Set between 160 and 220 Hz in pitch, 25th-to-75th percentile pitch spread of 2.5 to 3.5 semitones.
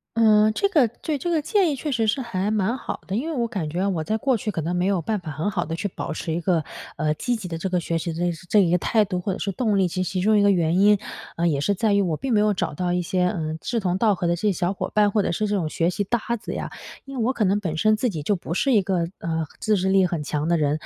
No: high, 190 Hz; average, 4.0 semitones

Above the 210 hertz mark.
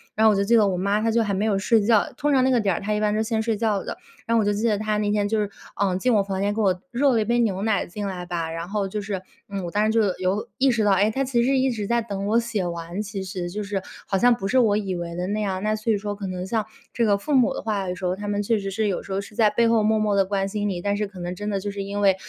No: high, 205 Hz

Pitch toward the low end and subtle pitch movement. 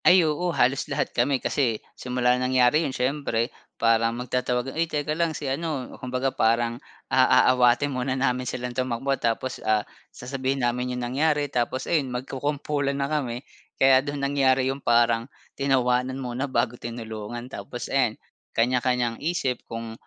Yes: low, 125 Hz; narrow, 2.2 semitones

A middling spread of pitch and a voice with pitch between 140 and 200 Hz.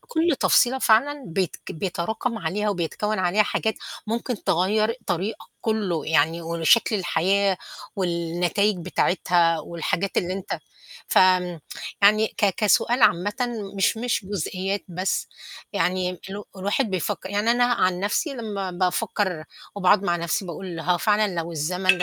Yes: average, 3.4 semitones; high, 190 Hz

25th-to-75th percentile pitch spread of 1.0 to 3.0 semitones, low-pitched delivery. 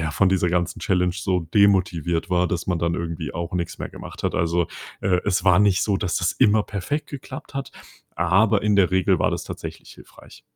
Yes: average, 2.7 semitones; very low, 90 Hz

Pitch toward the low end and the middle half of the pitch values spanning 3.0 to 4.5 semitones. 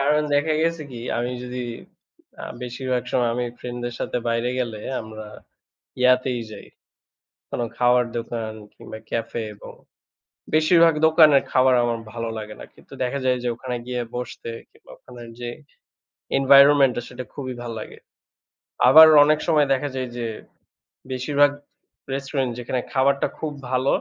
No: low, 125 Hz; narrow, 2.5 semitones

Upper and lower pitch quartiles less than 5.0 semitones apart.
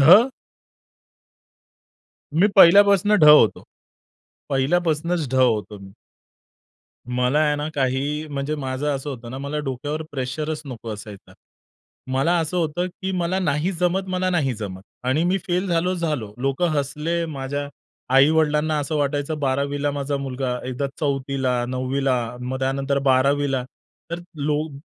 Yes: average, 3.3 semitones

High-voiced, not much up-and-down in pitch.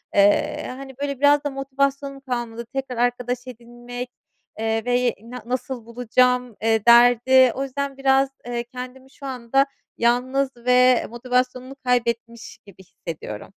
Yes: very high, 250 Hz; narrow, 2.0 semitones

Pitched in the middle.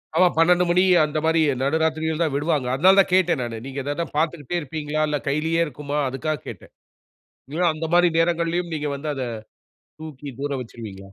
Yes: medium, 155 Hz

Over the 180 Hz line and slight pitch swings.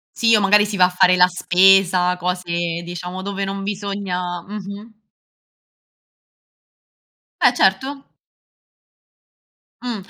Yes: high, 190 Hz; narrow, 2.2 semitones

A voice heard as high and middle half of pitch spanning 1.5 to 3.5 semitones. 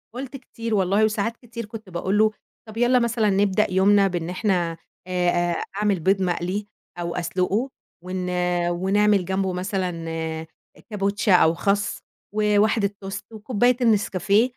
Yes: high, 200 Hz; average, 2.9 semitones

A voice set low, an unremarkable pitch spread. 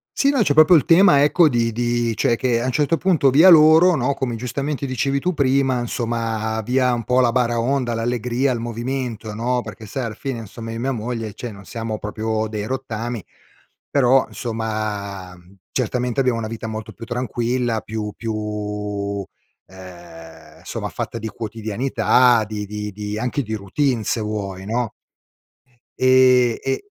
Yes: low, 115 Hz; average, 3.1 semitones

